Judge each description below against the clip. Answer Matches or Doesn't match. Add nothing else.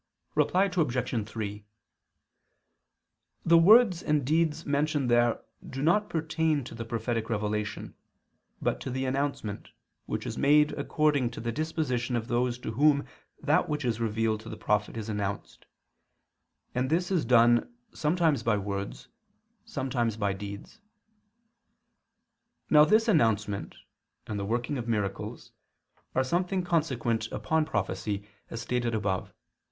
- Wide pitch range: Matches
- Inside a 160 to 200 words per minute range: Doesn't match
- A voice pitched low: Matches